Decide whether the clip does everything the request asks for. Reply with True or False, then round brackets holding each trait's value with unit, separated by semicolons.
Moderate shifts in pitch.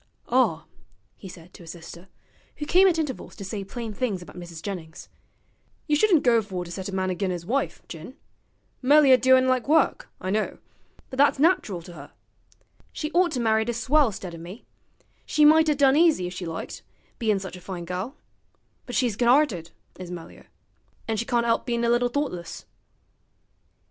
False (6.9 semitones)